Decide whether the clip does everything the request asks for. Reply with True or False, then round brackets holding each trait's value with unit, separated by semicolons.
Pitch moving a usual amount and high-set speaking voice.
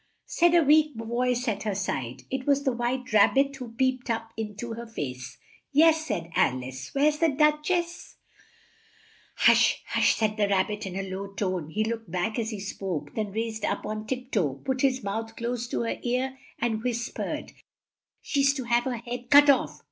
True (4.3 semitones; 235 Hz)